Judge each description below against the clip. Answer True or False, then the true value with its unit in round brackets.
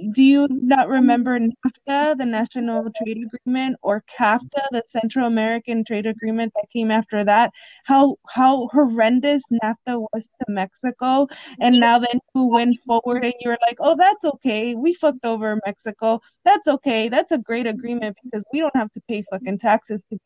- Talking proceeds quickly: False (170 wpm)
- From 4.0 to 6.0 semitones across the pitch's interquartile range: False (3.1 semitones)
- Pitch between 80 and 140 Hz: False (240 Hz)